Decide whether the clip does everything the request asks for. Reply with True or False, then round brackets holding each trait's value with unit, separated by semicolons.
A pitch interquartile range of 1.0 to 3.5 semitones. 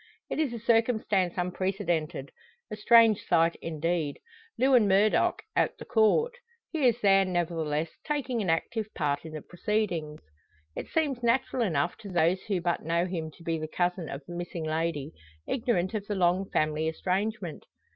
False (4.9 semitones)